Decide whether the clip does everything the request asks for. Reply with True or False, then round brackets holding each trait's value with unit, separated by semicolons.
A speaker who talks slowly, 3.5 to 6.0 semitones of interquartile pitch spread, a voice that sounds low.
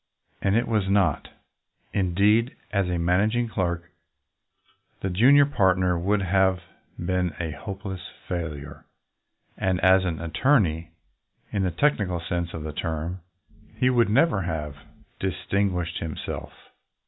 False (125 wpm; 3.0 semitones; 95 Hz)